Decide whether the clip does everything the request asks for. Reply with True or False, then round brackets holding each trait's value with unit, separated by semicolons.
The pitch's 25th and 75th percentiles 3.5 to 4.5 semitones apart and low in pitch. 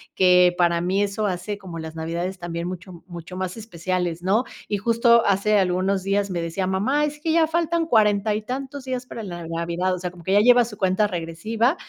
False (4.1 semitones; 190 Hz)